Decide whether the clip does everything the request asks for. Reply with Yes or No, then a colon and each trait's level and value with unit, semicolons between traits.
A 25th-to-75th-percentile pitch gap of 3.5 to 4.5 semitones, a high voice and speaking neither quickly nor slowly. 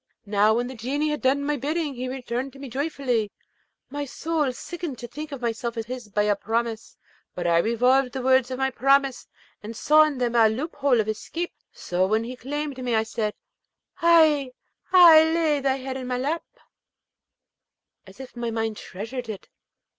Yes: average, 3.9 semitones; very high, 255 Hz; average, 180 wpm